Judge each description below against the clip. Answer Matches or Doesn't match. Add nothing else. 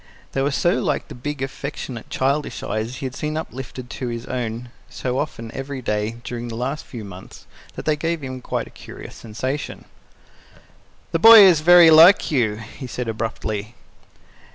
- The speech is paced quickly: Doesn't match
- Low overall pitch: Matches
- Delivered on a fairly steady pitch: Doesn't match